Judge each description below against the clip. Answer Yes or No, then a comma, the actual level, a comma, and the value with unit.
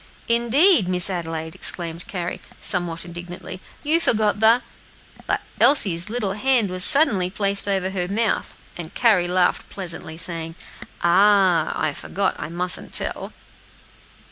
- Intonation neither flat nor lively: Yes, average, 3.7 semitones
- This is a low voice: No, medium, 185 Hz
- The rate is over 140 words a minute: No, slow, 135 wpm